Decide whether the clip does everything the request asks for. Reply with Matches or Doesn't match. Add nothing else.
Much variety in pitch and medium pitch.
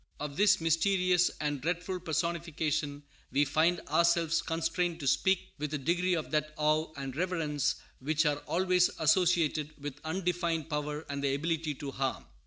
Doesn't match